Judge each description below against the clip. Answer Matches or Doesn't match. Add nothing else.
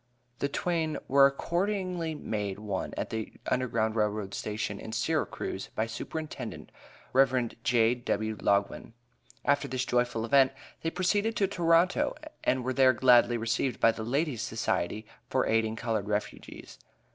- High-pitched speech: Doesn't match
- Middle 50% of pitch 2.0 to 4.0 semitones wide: Doesn't match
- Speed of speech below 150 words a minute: Matches